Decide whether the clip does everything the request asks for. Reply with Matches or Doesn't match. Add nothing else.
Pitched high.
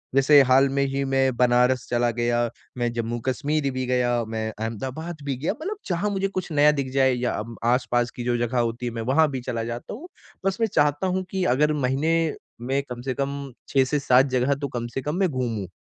Doesn't match